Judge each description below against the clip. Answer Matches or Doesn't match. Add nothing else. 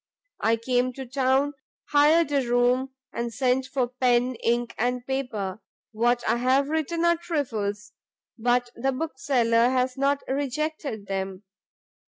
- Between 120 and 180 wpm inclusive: Matches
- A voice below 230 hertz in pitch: Doesn't match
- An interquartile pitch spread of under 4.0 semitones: Matches